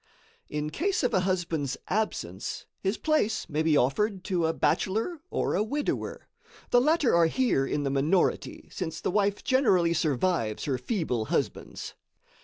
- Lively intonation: Yes, wide, 6.5 semitones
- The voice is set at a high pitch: No, medium, 180 Hz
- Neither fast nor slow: Yes, average, 155 wpm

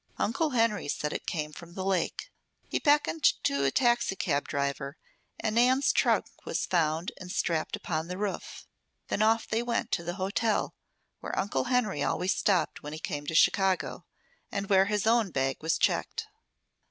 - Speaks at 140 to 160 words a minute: No, average, 170 wpm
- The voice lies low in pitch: No, high, 190 Hz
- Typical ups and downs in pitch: No, wide, 6.2 semitones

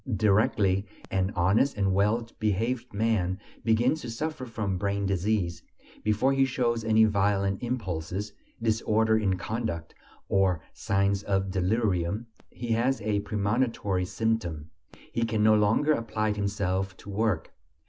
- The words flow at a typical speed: No, slow, 130 wpm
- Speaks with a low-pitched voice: Yes, low, 105 Hz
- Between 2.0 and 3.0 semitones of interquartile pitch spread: Yes, average, 2.7 semitones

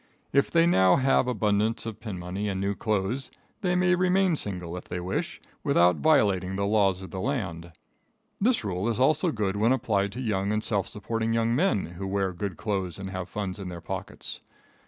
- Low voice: Yes, low, 105 Hz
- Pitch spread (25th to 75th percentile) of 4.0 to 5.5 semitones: Yes, average, 4.6 semitones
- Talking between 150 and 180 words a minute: No, average, 200 wpm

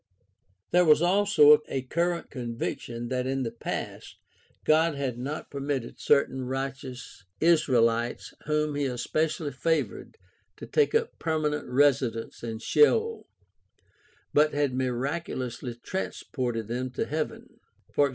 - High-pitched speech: No, medium, 140 Hz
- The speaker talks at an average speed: No, slow, 120 wpm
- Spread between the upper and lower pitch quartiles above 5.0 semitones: No, average, 3.8 semitones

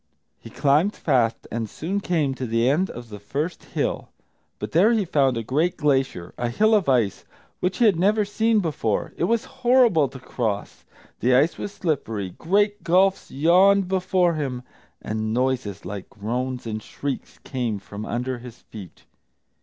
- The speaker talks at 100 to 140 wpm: No, average, 170 wpm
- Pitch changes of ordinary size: No, wide, 8.0 semitones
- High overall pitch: No, medium, 140 Hz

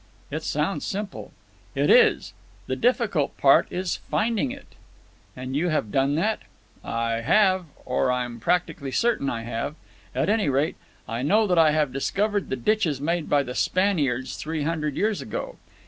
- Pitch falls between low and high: Yes, medium, 155 Hz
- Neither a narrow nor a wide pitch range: No, wide, 7.4 semitones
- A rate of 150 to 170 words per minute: Yes, average, 165 wpm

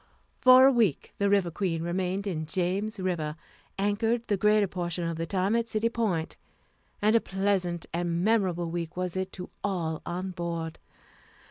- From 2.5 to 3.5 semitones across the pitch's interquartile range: Yes, average, 3.1 semitones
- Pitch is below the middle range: No, medium, 185 Hz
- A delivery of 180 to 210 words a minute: No, average, 165 wpm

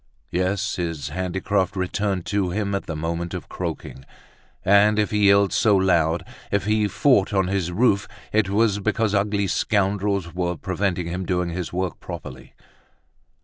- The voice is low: Yes, very low, 95 Hz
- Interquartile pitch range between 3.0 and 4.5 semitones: No, narrow, 2.4 semitones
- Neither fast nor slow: Yes, average, 155 wpm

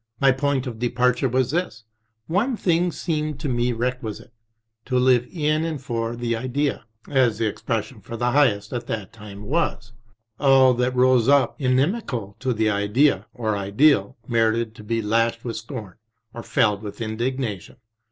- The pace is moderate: Yes, average, 170 wpm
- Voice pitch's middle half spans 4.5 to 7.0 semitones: No, average, 3.4 semitones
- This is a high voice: No, low, 120 Hz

